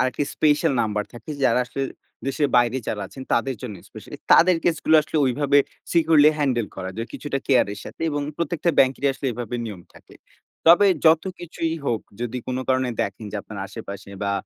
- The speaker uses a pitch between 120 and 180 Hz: Yes, low, 135 Hz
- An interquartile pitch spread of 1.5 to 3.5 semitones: No, average, 4.8 semitones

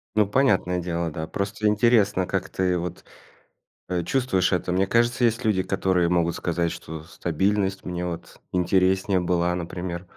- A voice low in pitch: Yes, very low, 90 Hz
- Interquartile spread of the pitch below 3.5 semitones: Yes, narrow, 2.5 semitones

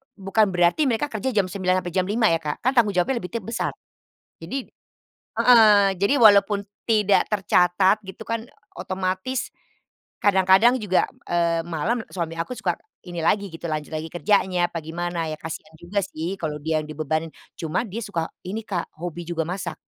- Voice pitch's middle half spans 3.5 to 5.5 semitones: Yes, average, 3.9 semitones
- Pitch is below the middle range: No, medium, 185 Hz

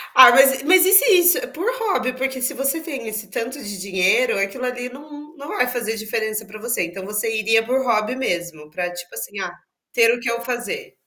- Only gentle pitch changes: No, average, 4.1 semitones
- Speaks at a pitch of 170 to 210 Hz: No, high, 245 Hz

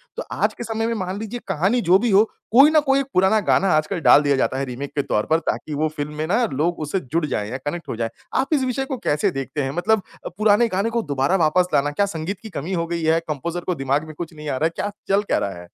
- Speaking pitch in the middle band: Yes, medium, 170 Hz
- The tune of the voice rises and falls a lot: Yes, wide, 6.2 semitones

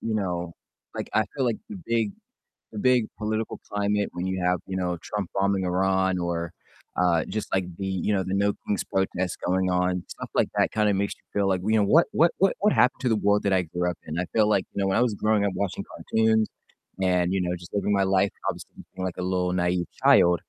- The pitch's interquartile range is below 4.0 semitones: Yes, average, 2.8 semitones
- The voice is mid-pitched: No, very low, 95 Hz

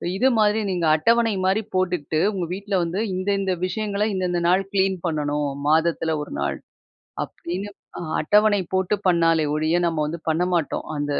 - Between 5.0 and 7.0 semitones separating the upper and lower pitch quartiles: No, average, 3.6 semitones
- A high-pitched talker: No, medium, 180 Hz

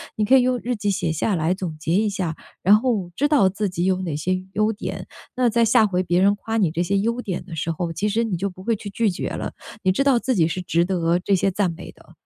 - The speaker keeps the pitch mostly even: No, average, 3.9 semitones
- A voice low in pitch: No, high, 195 Hz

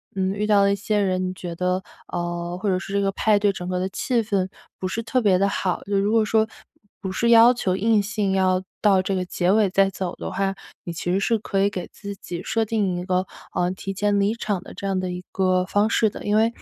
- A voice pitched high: Yes, high, 195 Hz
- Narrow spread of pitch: Yes, narrow, 2.3 semitones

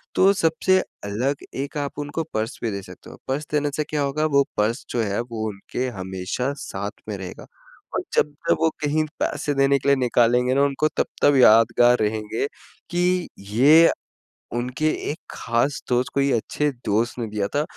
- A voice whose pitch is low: Yes, low, 130 Hz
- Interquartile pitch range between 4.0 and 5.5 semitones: Yes, average, 4.7 semitones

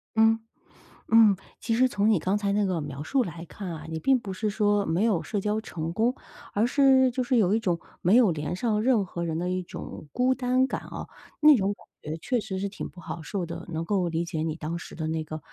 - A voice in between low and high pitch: No, high, 200 Hz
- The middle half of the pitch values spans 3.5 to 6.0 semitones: Yes, average, 5.1 semitones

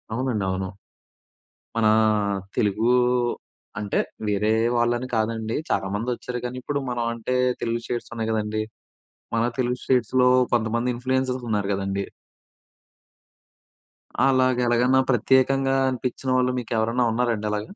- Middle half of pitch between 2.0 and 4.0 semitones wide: Yes, average, 2.7 semitones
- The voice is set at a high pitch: No, low, 120 Hz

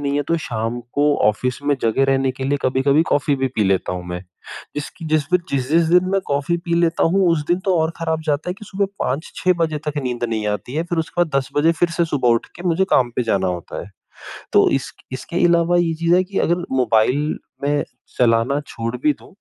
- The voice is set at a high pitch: No, medium, 145 Hz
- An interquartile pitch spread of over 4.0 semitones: Yes, average, 5.1 semitones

